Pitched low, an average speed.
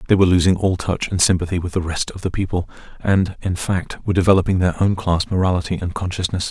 No: very low, 90 Hz; fast, 220 wpm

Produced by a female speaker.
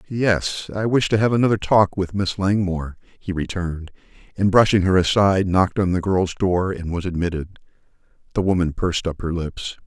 No: male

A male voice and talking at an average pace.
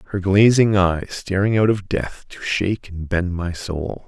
Yes: male; average, 190 wpm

